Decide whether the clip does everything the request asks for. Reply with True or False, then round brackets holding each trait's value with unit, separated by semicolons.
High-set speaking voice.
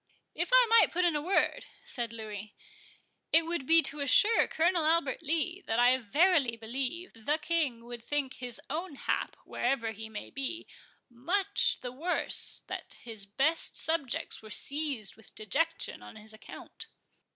True (280 Hz)